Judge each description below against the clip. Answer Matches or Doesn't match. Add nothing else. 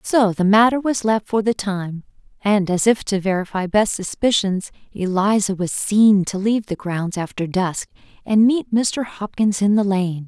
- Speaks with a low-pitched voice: Doesn't match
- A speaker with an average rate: Matches